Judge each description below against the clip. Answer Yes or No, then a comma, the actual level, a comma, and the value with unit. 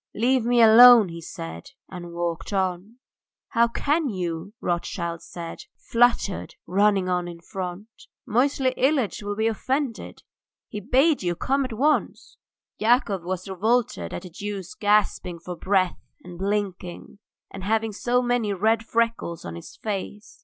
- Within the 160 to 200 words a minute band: No, average, 145 wpm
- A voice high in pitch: Yes, high, 205 Hz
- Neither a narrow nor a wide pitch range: Yes, average, 4.7 semitones